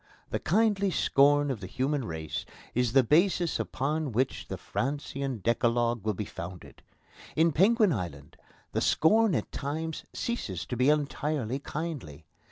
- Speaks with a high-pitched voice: No, medium, 140 Hz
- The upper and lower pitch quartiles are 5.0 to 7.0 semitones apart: Yes, wide, 5.4 semitones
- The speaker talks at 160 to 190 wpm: No, average, 145 wpm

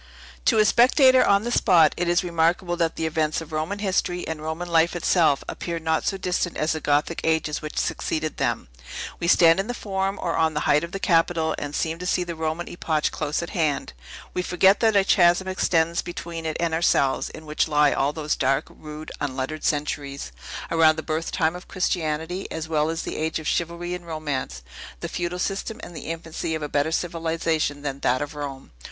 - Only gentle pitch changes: Yes, narrow, 2.3 semitones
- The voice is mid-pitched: Yes, medium, 165 Hz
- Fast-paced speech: Yes, fast, 210 wpm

